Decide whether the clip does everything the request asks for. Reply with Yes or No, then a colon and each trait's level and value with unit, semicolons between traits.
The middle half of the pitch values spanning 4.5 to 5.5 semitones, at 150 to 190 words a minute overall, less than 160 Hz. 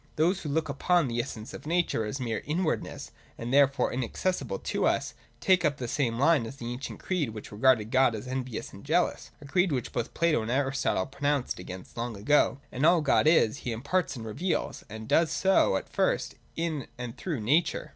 No: average, 5.2 semitones; fast, 205 wpm; low, 135 Hz